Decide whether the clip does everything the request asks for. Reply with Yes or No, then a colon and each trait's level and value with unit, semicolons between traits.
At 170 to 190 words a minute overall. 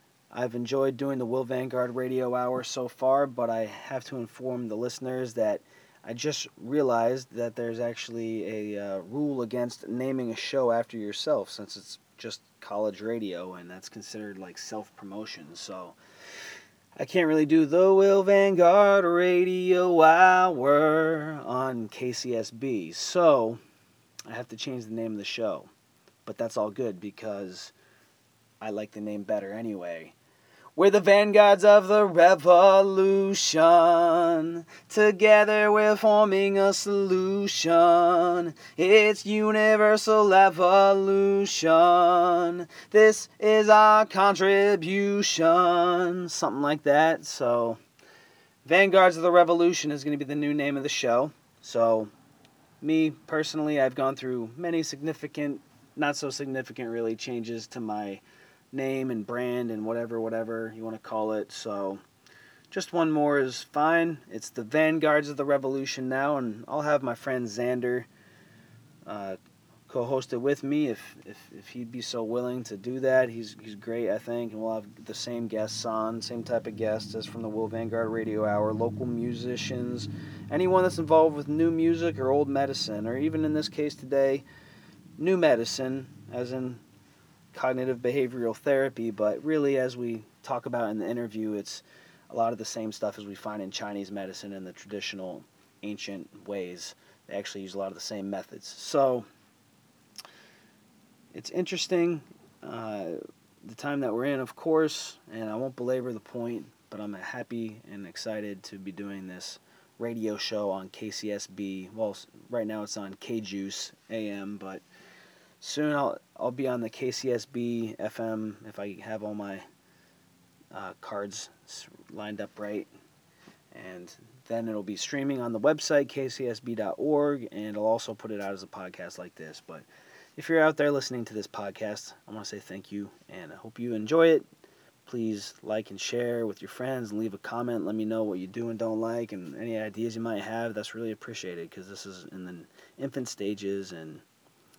No: average, 160 wpm